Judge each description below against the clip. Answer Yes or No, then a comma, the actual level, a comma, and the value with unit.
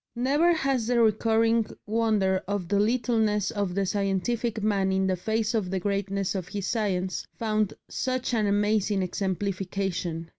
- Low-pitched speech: No, high, 205 Hz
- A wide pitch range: No, average, 2.8 semitones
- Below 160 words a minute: Yes, average, 150 wpm